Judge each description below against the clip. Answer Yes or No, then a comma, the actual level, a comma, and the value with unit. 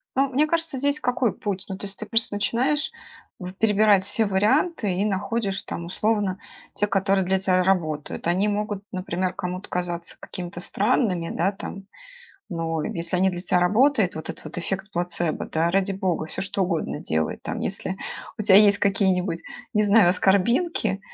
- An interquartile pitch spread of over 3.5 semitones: No, average, 2.9 semitones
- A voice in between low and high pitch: No, high, 195 Hz